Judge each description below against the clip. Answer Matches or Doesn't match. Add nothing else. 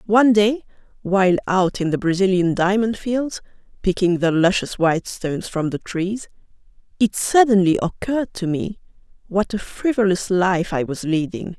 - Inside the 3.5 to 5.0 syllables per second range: Matches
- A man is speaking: Doesn't match